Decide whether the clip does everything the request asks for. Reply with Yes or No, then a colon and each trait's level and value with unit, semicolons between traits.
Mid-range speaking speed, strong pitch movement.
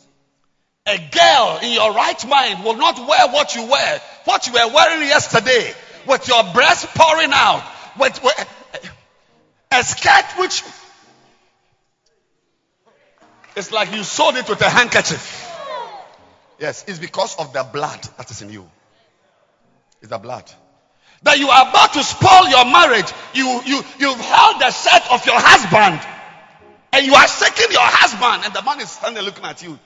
Yes: average, 160 wpm; wide, 9.0 semitones